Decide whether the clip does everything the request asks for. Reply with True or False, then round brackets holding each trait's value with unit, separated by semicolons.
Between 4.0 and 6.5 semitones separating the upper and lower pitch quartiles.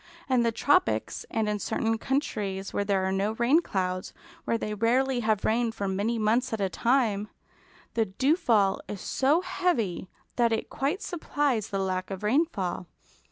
True (4.8 semitones)